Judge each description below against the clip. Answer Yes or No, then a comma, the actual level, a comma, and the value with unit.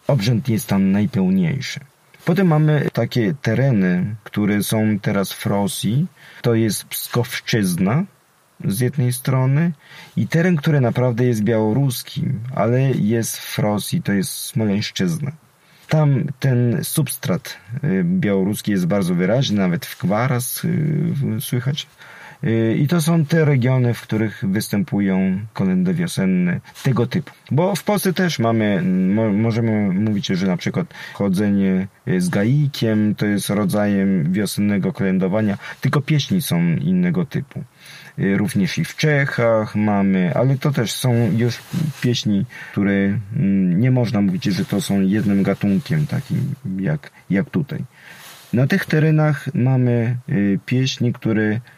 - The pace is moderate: Yes, average, 125 wpm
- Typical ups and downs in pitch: No, wide, 7.0 semitones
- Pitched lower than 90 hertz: No, low, 130 Hz